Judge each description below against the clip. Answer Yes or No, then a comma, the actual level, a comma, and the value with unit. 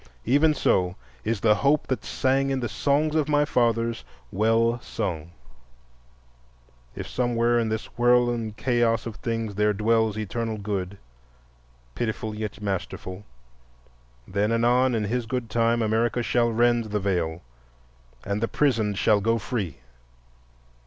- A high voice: No, low, 115 Hz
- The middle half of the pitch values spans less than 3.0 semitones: Yes, narrow, 2.5 semitones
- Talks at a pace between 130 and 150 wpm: Yes, average, 140 wpm